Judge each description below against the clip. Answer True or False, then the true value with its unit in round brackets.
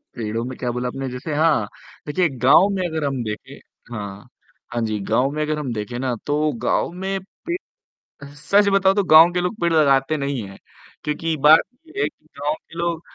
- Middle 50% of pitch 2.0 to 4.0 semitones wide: False (5.2 semitones)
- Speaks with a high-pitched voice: False (150 Hz)